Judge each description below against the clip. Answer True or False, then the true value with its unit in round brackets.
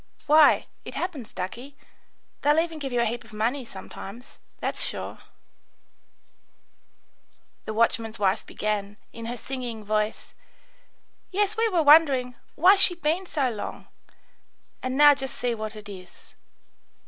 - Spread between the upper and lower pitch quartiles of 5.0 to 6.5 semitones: True (5.3 semitones)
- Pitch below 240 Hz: False (245 Hz)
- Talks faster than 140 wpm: False (135 wpm)